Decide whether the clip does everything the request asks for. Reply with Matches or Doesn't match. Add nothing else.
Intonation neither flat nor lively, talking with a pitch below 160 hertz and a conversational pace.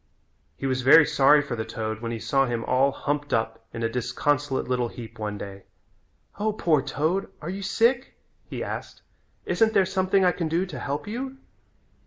Doesn't match